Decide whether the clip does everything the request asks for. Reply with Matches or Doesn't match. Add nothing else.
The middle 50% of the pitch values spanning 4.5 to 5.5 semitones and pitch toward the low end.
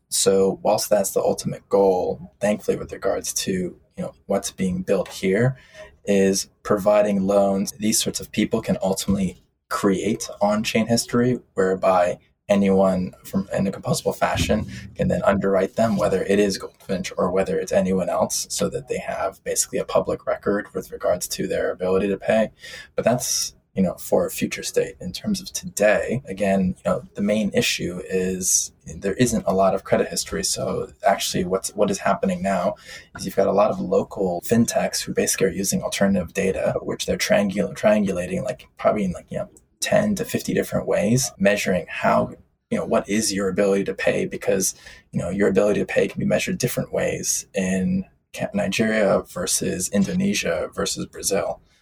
Matches